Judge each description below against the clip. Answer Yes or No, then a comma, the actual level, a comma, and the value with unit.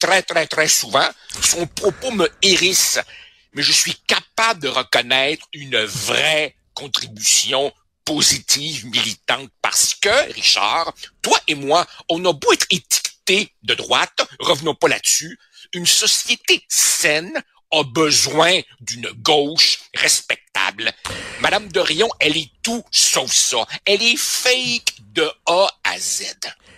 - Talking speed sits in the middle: No, slow, 130 wpm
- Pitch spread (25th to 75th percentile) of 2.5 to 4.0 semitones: No, average, 5.0 semitones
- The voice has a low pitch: No, medium, 165 Hz